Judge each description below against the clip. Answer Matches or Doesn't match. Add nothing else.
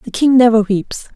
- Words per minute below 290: Matches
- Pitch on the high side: Matches